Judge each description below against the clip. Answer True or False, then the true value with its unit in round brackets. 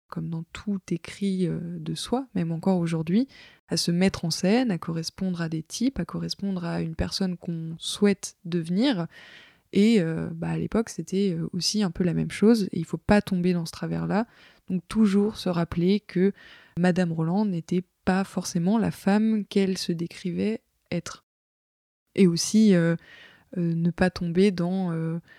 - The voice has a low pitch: False (180 Hz)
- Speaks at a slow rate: False (175 wpm)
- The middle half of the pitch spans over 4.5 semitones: False (2.8 semitones)